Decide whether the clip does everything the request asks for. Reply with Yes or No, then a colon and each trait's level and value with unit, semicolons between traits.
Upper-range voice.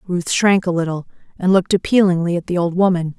No: medium, 180 Hz